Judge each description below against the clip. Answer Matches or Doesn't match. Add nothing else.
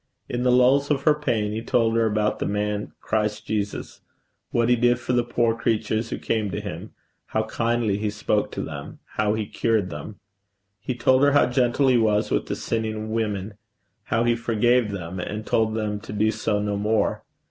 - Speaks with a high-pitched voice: Doesn't match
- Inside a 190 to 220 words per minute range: Matches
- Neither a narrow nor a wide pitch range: Doesn't match